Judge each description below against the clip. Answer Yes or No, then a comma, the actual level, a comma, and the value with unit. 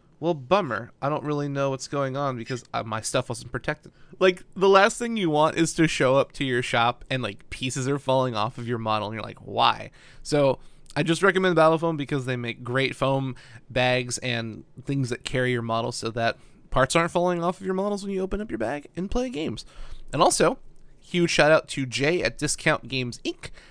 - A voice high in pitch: No, low, 135 Hz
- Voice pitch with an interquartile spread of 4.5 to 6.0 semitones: Yes, average, 5.3 semitones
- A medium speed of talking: No, fast, 220 wpm